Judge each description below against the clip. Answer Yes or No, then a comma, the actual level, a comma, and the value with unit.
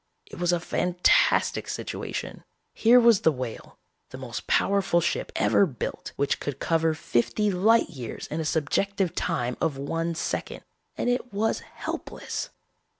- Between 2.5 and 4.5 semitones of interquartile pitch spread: No, wide, 5.4 semitones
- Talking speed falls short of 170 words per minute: Yes, average, 150 wpm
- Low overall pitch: No, medium, 170 Hz